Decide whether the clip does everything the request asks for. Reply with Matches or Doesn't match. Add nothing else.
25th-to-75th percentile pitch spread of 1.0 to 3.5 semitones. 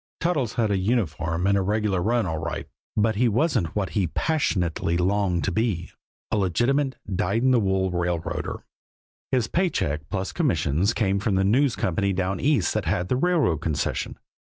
Doesn't match